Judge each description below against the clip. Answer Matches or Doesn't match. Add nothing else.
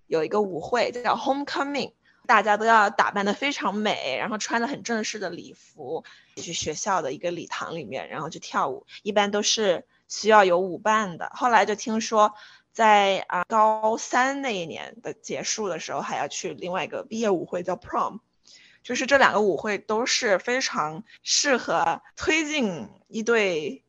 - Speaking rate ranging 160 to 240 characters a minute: Doesn't match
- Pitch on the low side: Doesn't match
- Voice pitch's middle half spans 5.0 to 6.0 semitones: Doesn't match